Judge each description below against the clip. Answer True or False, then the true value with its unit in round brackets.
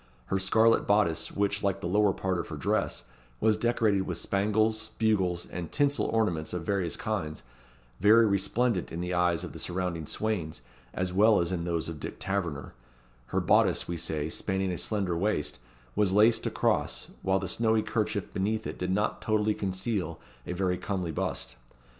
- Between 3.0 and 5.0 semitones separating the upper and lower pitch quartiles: True (3.5 semitones)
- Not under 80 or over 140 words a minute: False (175 wpm)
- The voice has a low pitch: True (95 Hz)